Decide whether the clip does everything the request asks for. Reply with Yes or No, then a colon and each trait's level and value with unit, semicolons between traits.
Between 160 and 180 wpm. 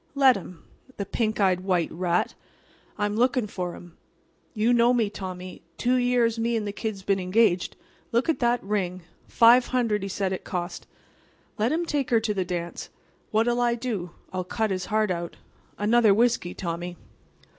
Yes: average, 175 wpm